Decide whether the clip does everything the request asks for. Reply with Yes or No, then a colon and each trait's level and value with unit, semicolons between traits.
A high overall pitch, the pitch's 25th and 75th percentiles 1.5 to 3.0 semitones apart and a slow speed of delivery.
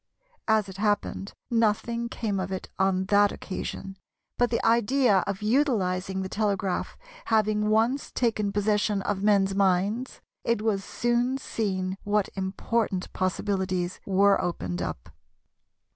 Yes: high, 205 Hz; average, 2.7 semitones; slow, 130 wpm